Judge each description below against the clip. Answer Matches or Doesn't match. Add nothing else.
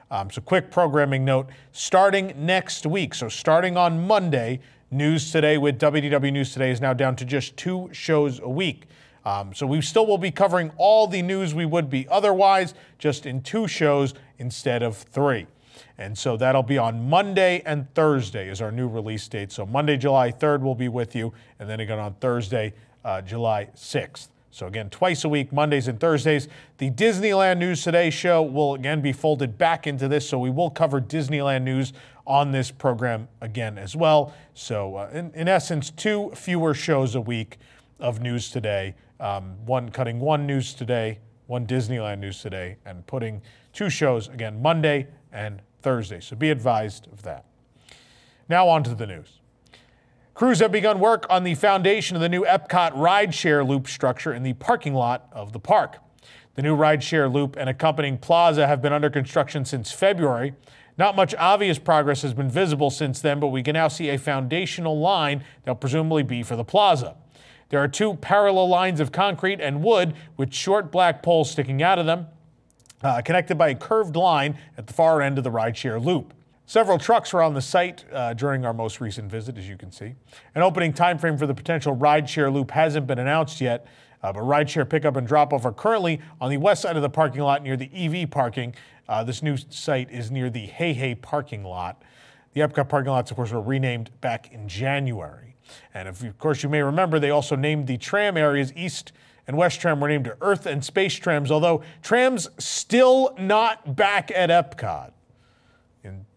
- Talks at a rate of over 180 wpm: Matches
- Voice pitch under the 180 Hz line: Matches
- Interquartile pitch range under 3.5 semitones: Doesn't match